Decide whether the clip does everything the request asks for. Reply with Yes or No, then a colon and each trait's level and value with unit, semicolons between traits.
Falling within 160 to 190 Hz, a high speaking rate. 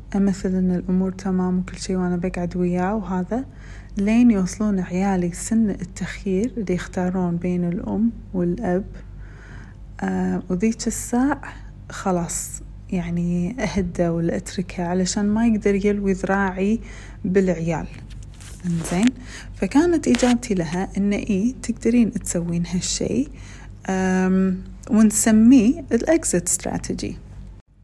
No: medium, 185 Hz; average, 95 wpm